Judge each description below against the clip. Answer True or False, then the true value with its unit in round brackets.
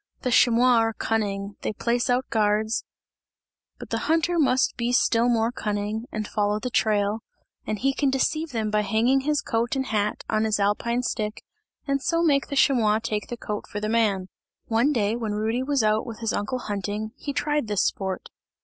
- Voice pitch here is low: False (225 Hz)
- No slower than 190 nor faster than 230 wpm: True (195 wpm)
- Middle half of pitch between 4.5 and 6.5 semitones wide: False (3.3 semitones)